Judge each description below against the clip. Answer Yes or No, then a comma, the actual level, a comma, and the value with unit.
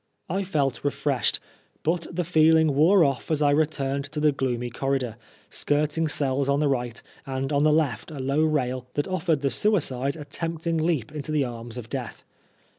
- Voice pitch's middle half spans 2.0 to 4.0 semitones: Yes, average, 2.9 semitones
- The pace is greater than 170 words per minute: Yes, average, 185 wpm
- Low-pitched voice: No, medium, 145 Hz